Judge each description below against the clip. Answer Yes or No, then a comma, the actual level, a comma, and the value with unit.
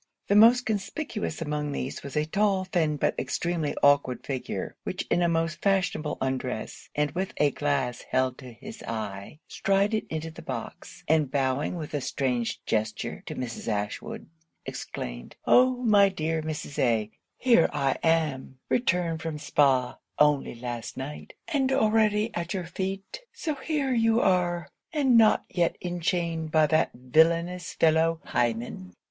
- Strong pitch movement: Yes, wide, 6.5 semitones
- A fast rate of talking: No, average, 150 wpm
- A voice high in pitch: No, medium, 160 Hz